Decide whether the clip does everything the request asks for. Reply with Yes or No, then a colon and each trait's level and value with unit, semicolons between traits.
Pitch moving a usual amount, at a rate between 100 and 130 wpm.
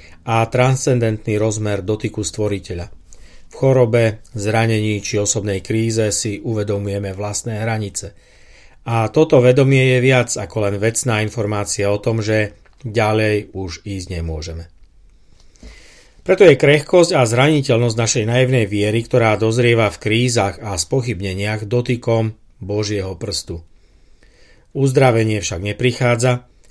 Yes: average, 3.1 semitones; average, 115 wpm